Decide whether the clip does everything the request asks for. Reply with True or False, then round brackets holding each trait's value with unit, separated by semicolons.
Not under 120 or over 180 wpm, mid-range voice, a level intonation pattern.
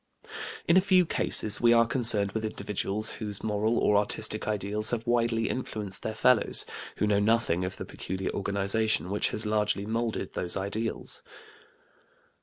False (155 wpm; 110 Hz; 2.3 semitones)